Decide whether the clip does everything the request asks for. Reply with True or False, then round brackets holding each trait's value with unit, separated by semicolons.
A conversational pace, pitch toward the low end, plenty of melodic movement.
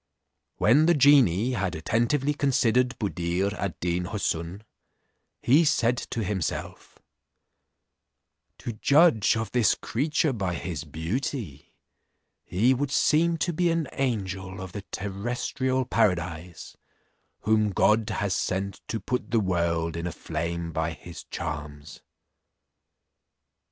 False (120 wpm; 105 Hz; 6.7 semitones)